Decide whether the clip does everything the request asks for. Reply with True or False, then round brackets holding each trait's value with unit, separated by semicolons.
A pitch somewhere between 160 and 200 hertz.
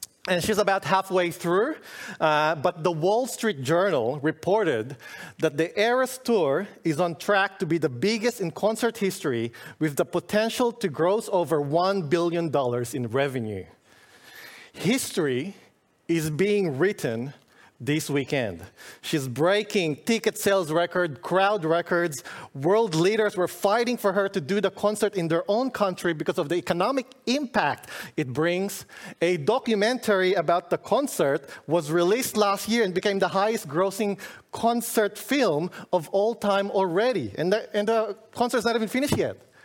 True (190 Hz)